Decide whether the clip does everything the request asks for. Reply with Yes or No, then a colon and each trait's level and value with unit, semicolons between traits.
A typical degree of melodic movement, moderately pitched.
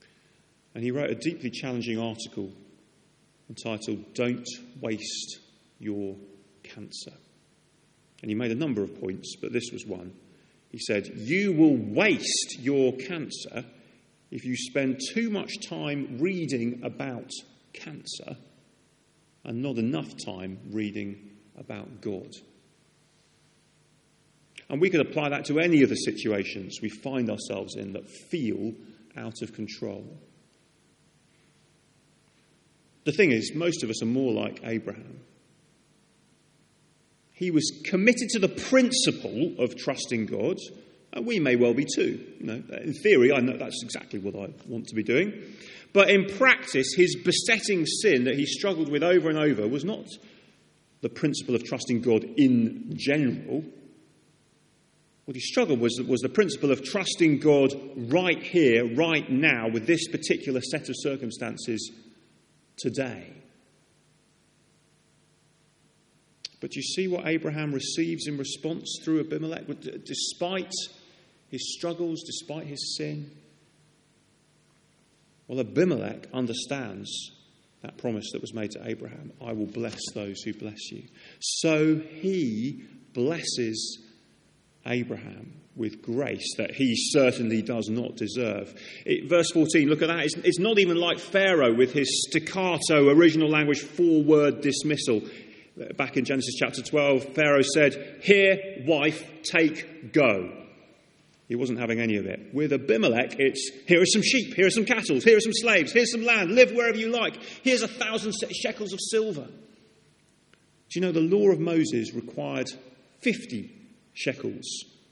No: wide, 6.8 semitones; medium, 145 Hz